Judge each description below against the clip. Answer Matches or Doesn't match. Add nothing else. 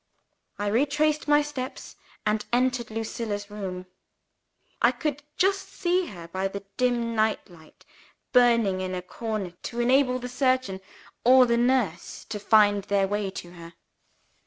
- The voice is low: Doesn't match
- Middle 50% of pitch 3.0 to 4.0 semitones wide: Doesn't match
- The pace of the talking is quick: Doesn't match